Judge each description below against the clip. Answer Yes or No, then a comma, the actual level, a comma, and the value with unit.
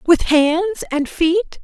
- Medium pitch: No, very high, 340 Hz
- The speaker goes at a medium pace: Yes, average, 145 wpm